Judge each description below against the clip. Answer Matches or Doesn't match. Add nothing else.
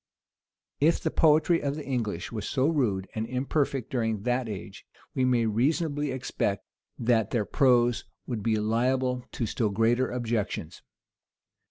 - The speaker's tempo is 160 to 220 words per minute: Doesn't match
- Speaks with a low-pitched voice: Matches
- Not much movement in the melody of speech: Doesn't match